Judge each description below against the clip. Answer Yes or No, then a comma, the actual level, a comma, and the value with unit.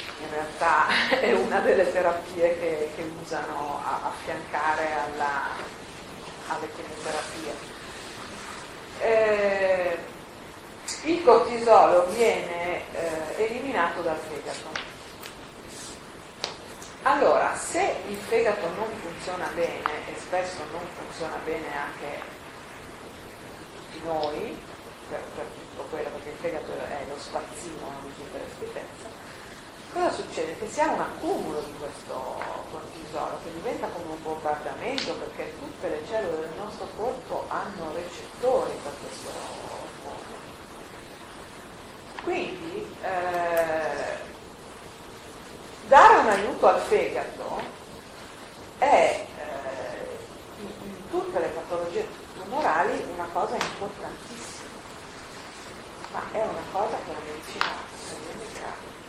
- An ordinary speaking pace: No, slow, 105 wpm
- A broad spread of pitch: Yes, wide, 6.5 semitones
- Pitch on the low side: No, medium, 180 Hz